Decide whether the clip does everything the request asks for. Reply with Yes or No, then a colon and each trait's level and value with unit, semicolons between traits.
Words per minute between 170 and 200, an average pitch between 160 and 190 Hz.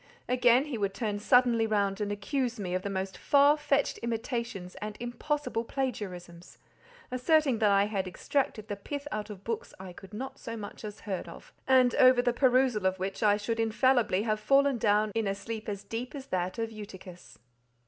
No: average, 190 wpm; high, 220 Hz